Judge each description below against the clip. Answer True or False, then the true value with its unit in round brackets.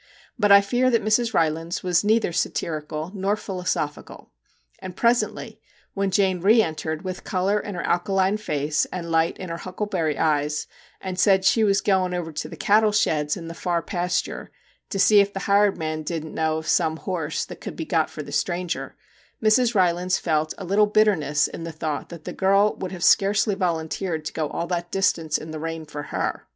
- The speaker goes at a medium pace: False (210 wpm)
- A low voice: False (180 Hz)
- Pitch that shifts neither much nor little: True (3.8 semitones)